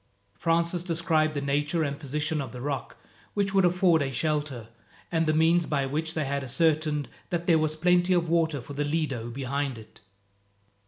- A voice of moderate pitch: Yes, medium, 155 Hz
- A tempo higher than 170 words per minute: Yes, average, 180 wpm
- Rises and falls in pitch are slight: No, average, 3.1 semitones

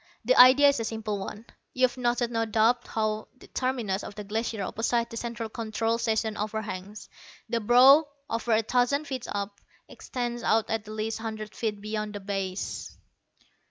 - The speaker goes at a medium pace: Yes, average, 170 wpm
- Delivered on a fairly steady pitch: Yes, narrow, 2.1 semitones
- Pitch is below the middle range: No, high, 225 Hz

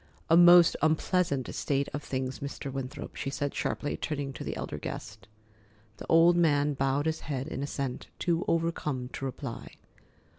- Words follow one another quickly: No, average, 160 wpm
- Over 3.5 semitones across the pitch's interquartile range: No, average, 3.2 semitones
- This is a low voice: No, medium, 145 Hz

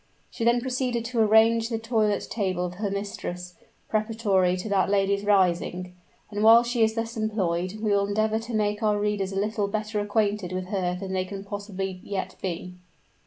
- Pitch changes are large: No, narrow, 2.6 semitones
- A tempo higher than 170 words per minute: Yes, average, 185 wpm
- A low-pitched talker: No, high, 205 Hz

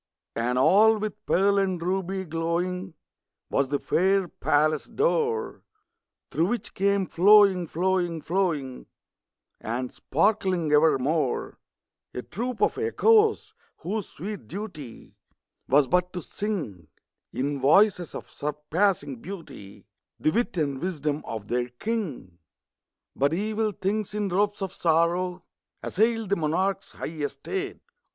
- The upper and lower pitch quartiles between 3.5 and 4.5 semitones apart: No, average, 5.3 semitones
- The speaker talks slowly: Yes, slow, 120 wpm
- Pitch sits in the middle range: Yes, medium, 180 Hz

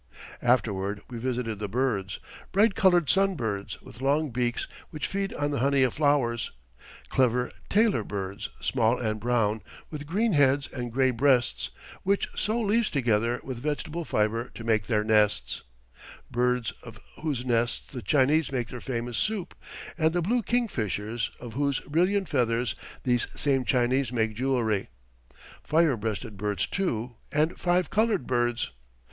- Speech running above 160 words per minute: No, average, 150 wpm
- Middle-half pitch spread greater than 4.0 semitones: Yes, average, 5.1 semitones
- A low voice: Yes, low, 125 Hz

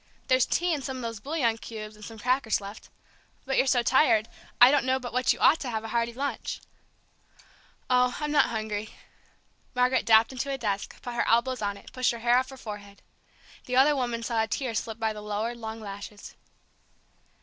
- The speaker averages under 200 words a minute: No, fast, 205 wpm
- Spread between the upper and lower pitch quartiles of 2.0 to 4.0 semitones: Yes, average, 2.9 semitones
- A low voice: No, high, 235 Hz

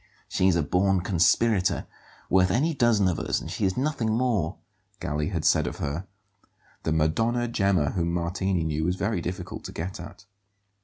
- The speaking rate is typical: Yes, average, 170 wpm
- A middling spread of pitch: Yes, average, 4.4 semitones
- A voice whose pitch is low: Yes, very low, 95 Hz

